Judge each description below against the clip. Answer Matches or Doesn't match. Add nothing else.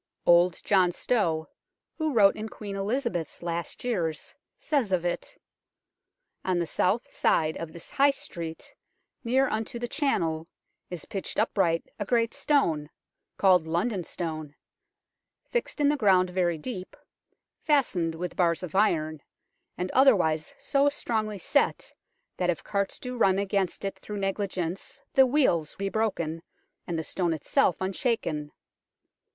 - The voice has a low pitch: Doesn't match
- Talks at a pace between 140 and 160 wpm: Matches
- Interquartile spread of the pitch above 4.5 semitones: Matches